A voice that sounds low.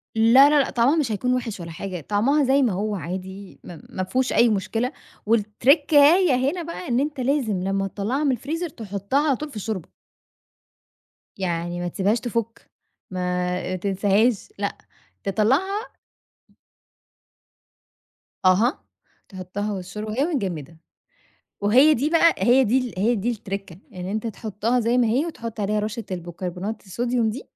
No: high, 220 Hz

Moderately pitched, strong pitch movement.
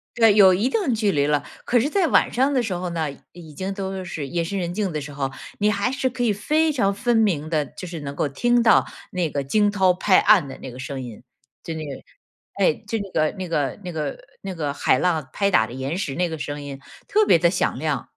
Yes: medium, 180 Hz; wide, 6.2 semitones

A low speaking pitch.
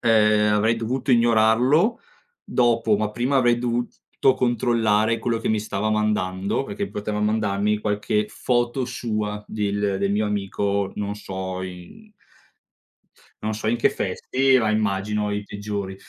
Yes: low, 105 Hz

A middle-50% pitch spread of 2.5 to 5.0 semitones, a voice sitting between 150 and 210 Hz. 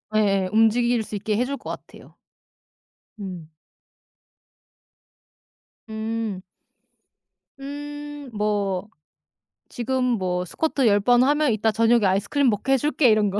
No: average, 4.3 semitones; high, 225 Hz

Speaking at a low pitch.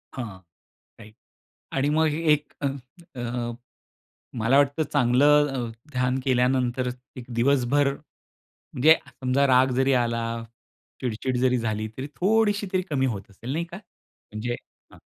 Yes: low, 130 Hz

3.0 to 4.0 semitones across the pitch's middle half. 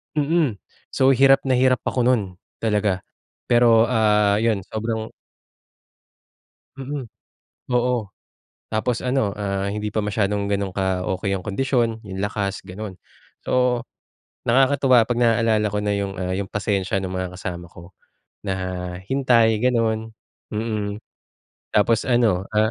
Yes: average, 3.6 semitones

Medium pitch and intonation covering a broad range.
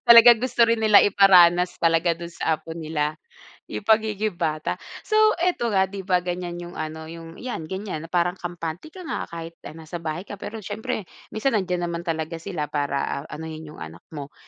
No: medium, 175 Hz; average, 4.1 semitones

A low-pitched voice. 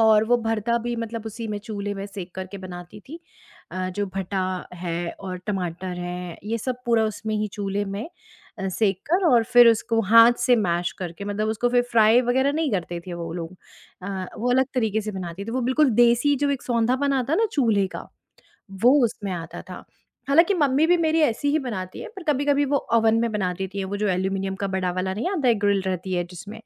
No: high, 215 Hz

